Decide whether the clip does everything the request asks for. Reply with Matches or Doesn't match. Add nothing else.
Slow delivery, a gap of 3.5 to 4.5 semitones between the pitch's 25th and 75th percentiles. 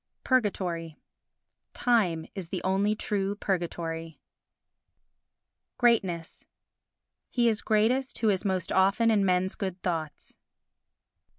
Matches